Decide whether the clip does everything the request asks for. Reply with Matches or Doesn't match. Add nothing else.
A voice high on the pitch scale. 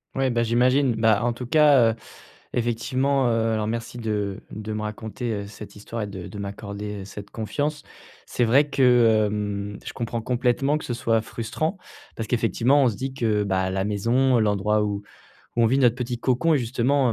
Doesn't match